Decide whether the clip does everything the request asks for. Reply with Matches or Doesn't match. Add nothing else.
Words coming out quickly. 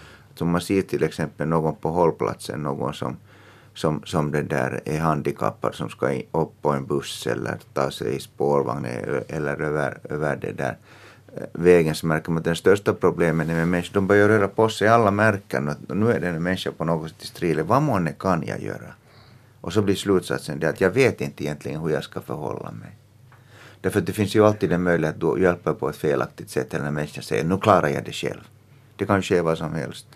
Matches